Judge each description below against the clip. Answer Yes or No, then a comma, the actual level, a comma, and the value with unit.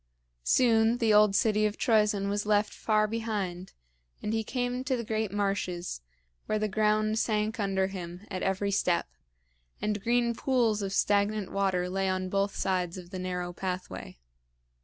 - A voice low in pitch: No, high, 205 Hz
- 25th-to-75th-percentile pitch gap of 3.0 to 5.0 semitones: No, narrow, 2.4 semitones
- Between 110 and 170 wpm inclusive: Yes, average, 160 wpm